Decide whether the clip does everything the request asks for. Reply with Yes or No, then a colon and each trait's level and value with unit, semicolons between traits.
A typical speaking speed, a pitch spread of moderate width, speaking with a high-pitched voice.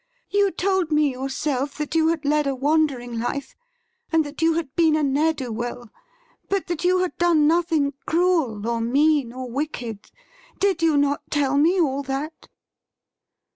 Yes: average, 170 wpm; average, 3.5 semitones; very high, 295 Hz